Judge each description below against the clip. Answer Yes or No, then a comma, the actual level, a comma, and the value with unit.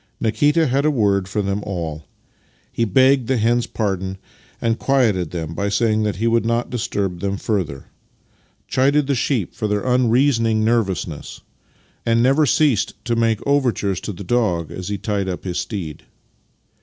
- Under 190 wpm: Yes, average, 165 wpm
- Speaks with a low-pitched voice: Yes, low, 110 Hz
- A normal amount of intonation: Yes, average, 4.1 semitones